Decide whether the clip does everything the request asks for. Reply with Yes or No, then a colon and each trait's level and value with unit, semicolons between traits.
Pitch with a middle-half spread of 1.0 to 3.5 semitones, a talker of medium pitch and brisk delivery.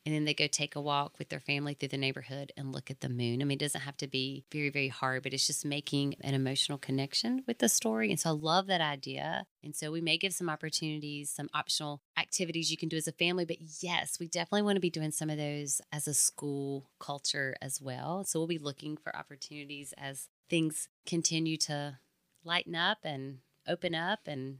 Yes: average, 2.9 semitones; medium, 150 Hz; fast, 225 wpm